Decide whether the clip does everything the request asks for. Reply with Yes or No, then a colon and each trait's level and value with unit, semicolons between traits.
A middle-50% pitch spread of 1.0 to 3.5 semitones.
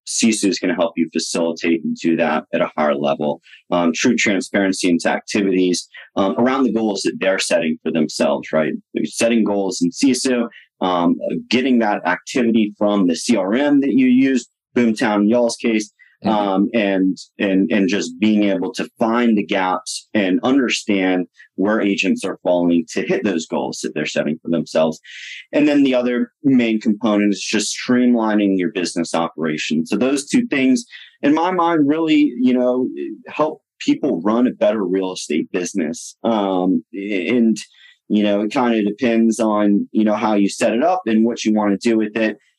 No: average, 4.6 semitones